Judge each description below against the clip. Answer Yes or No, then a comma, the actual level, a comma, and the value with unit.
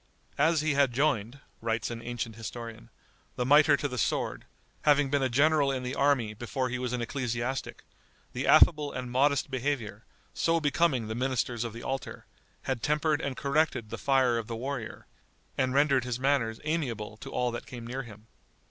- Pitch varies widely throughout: No, average, 3.3 semitones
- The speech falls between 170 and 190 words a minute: Yes, average, 185 wpm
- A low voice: Yes, low, 130 Hz